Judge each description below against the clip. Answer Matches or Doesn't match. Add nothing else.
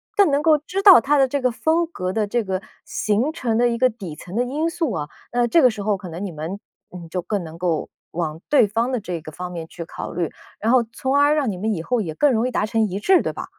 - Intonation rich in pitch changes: Matches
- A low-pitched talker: Doesn't match